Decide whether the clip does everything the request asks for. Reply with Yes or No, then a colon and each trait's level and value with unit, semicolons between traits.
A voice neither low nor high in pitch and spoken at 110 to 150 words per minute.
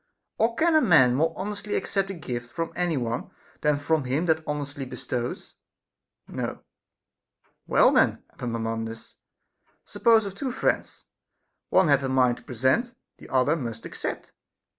Yes: medium, 145 Hz; average, 145 wpm